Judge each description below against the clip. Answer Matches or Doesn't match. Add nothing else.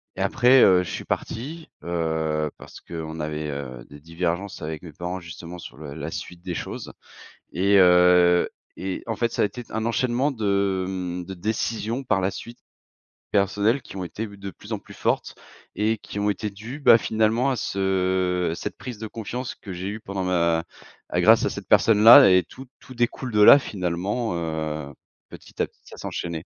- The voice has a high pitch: Doesn't match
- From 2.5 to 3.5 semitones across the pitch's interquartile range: Doesn't match